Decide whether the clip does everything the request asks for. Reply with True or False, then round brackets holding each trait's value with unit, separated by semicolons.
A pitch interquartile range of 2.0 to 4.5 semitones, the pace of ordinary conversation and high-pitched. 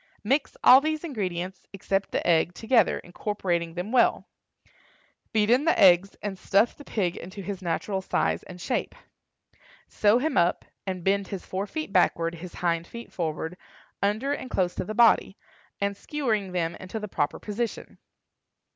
True (4.2 semitones; 165 wpm; 195 Hz)